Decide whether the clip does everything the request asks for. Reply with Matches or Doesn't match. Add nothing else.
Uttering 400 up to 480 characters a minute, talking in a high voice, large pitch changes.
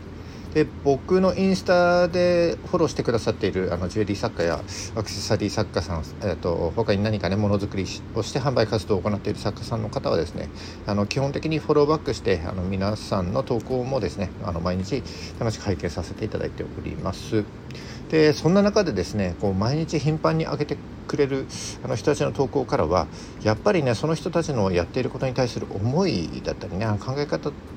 Doesn't match